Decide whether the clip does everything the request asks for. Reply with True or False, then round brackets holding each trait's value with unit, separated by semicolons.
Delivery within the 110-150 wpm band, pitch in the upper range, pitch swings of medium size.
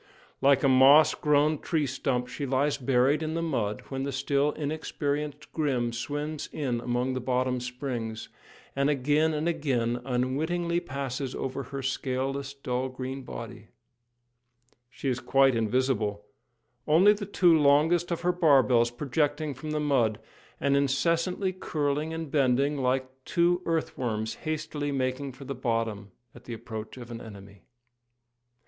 False (145 wpm; 135 Hz; 3.3 semitones)